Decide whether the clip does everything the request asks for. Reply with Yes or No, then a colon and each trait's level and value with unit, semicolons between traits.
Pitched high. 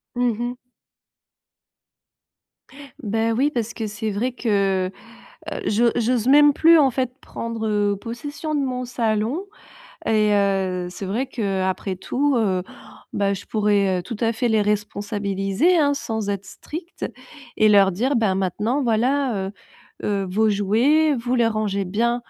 Yes: high, 220 Hz